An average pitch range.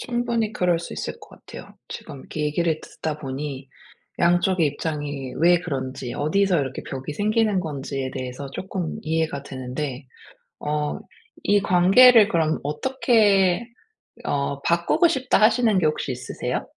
No: wide, 5.9 semitones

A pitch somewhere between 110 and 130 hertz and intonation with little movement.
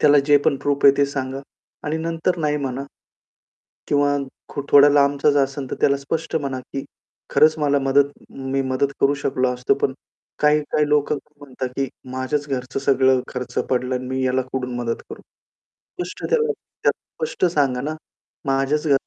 No: medium, 140 Hz; narrow, 1.9 semitones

